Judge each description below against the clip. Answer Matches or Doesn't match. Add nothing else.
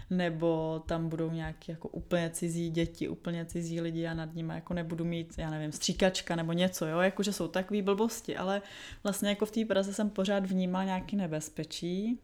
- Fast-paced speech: Matches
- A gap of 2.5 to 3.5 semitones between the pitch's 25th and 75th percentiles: Matches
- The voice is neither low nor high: Matches